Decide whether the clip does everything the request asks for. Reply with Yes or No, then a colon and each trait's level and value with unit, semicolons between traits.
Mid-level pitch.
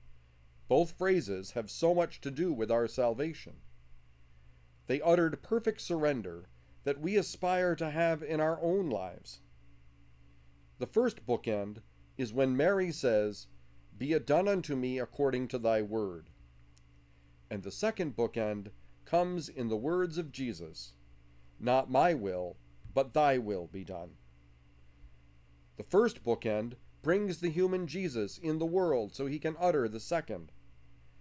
No: low, 115 Hz